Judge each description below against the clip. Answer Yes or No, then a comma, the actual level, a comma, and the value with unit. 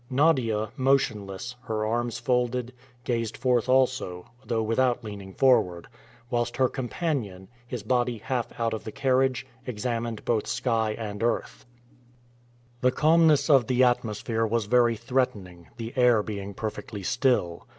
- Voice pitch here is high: No, low, 120 Hz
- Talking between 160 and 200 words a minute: No, slow, 135 wpm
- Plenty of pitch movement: No, average, 2.8 semitones